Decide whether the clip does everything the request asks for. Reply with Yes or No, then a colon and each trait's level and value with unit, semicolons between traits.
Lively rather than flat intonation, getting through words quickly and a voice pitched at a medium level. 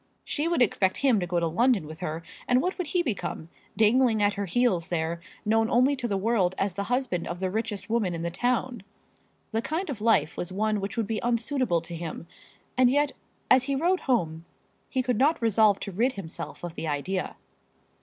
No: wide, 6.0 semitones; fast, 210 wpm; high, 215 Hz